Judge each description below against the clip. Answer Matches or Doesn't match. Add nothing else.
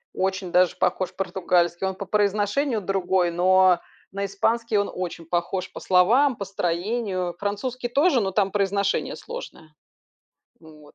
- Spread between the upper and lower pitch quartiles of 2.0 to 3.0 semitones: Matches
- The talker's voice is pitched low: Doesn't match